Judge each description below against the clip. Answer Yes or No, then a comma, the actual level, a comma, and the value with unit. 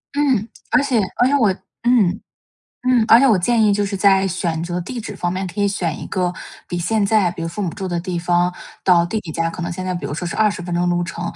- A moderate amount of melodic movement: Yes, average, 3.6 semitones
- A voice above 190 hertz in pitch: No, medium, 185 Hz